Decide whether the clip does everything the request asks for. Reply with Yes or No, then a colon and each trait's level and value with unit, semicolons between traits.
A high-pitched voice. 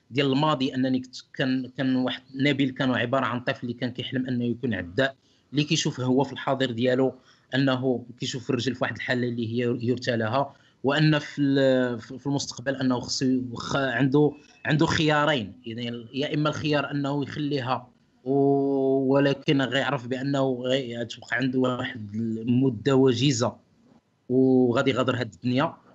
No: low, 130 Hz